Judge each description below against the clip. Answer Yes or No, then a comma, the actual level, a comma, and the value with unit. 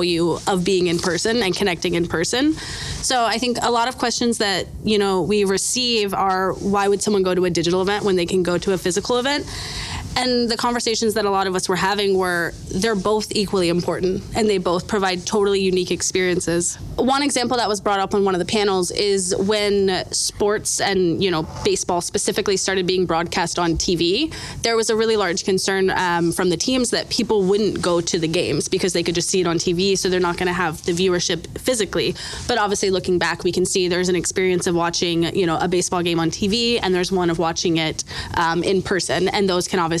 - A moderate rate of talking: No, fast, 225 wpm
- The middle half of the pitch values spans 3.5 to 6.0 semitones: No, average, 2.7 semitones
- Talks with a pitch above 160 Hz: Yes, high, 190 Hz